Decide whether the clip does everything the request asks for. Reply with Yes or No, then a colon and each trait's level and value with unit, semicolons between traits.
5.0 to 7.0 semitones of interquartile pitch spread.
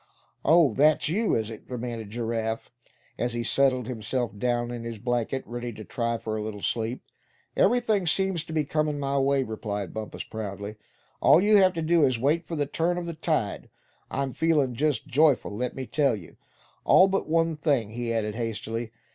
Yes: wide, 5.4 semitones